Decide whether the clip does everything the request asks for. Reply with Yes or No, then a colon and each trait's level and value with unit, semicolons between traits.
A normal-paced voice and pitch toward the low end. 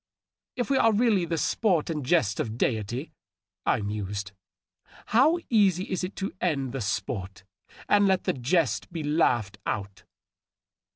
No: average, 160 wpm; medium, 150 Hz